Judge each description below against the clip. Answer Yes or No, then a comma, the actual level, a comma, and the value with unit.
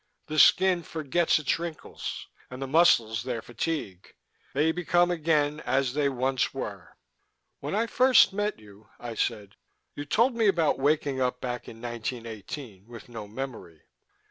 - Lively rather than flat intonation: Yes, wide, 5.8 semitones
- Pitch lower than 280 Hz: Yes, low, 135 Hz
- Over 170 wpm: No, average, 150 wpm